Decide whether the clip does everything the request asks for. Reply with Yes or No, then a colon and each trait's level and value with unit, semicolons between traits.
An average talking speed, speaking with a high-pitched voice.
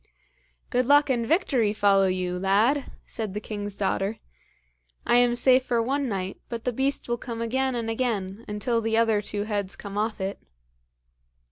Yes: average, 170 wpm; high, 225 Hz